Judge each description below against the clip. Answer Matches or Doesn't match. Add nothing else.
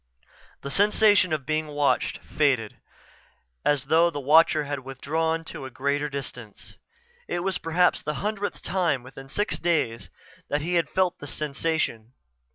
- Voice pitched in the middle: Matches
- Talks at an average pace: Matches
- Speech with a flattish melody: Doesn't match